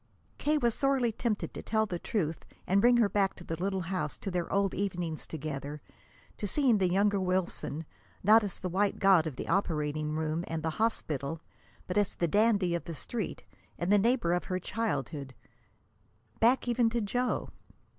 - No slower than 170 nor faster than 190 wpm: Yes, average, 185 wpm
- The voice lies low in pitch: No, high, 190 Hz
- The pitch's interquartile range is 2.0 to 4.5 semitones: No, average, 5.0 semitones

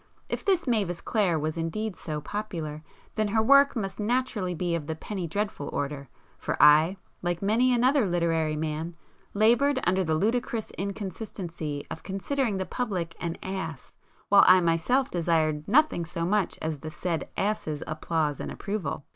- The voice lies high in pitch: No, medium, 180 Hz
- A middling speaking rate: Yes, average, 160 wpm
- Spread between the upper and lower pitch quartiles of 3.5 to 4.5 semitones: No, average, 5.1 semitones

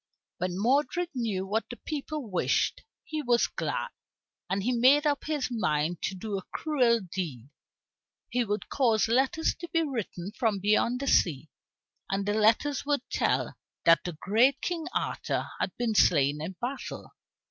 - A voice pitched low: No, high, 225 Hz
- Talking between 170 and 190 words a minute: No, average, 160 wpm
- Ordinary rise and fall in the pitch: No, wide, 6.3 semitones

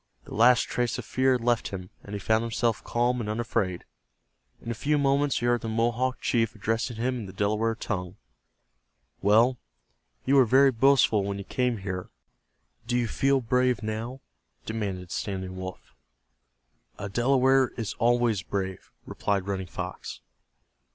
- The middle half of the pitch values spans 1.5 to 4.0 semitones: Yes, average, 3.7 semitones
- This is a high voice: No, low, 115 Hz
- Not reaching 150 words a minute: No, average, 160 wpm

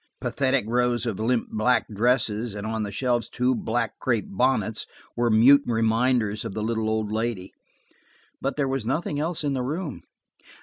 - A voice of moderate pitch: No, low, 120 Hz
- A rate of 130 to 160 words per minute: No, average, 170 wpm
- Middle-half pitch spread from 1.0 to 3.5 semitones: Yes, average, 2.9 semitones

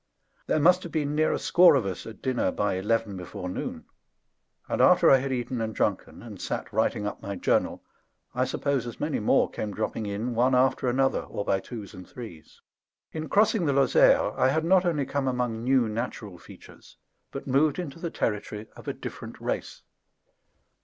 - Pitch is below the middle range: Yes, low, 125 Hz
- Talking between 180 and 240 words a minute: Yes, average, 190 wpm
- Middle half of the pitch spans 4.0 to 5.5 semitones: Yes, average, 4.9 semitones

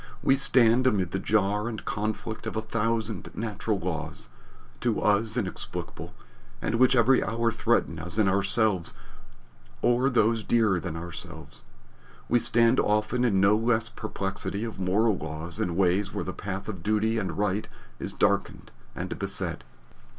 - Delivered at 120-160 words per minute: Yes, average, 150 wpm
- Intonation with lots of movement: No, average, 3.3 semitones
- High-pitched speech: No, low, 105 Hz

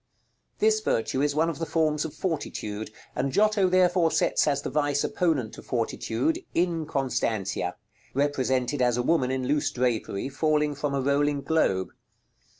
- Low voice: No, medium, 145 Hz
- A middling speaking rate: Yes, average, 150 wpm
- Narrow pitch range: No, average, 4.1 semitones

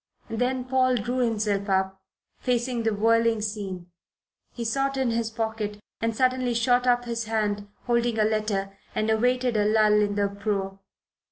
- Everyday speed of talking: Yes, average, 160 wpm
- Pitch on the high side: Yes, high, 225 Hz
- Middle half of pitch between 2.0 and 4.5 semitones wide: Yes, average, 2.7 semitones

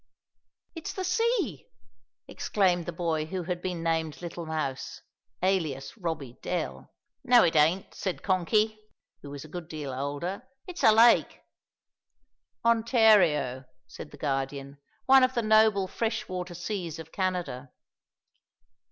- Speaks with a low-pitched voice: No, medium, 175 Hz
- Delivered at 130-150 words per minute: Yes, slow, 135 wpm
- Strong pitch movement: Yes, wide, 5.9 semitones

